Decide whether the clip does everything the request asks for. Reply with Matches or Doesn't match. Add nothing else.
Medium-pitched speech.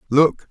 Matches